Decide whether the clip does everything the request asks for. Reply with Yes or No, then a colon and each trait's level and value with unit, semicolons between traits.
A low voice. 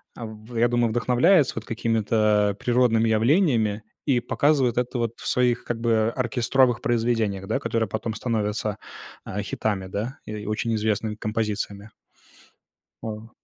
Yes: low, 115 Hz